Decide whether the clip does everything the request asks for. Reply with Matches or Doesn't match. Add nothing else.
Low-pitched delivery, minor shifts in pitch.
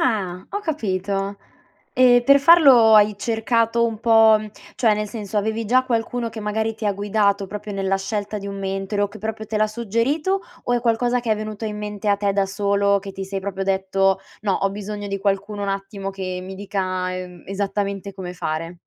Doesn't match